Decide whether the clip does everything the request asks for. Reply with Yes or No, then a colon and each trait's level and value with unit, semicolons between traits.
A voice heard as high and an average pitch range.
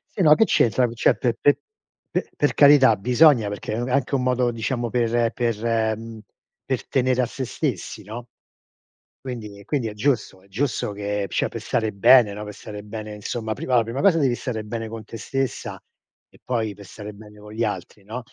No: low, 115 Hz; average, 3.1 semitones